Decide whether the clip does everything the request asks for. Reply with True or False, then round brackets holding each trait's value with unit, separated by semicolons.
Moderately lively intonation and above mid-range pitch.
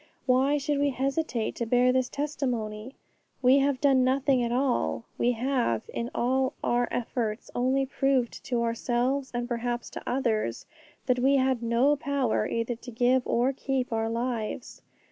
False (2.3 semitones; 250 Hz)